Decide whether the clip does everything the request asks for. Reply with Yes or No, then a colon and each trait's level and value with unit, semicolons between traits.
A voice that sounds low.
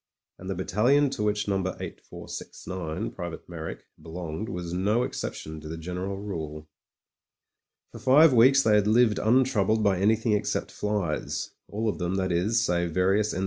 Yes: low, 100 Hz